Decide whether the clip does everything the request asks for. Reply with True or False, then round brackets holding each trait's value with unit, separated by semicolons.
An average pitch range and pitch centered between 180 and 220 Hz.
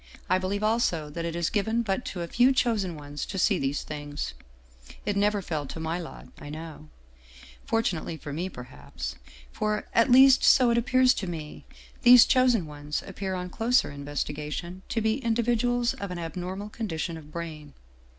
False (6.7 semitones; 185 Hz)